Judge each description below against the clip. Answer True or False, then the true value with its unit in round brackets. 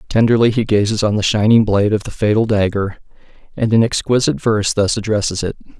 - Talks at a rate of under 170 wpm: False (185 wpm)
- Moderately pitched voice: False (105 Hz)